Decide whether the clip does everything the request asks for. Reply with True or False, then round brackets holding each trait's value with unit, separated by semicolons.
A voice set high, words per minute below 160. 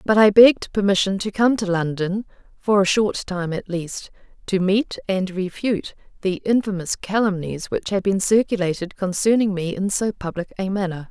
False (195 Hz; 175 wpm)